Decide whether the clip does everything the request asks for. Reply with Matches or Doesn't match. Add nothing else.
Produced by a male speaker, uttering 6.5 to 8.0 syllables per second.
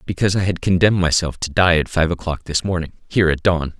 Matches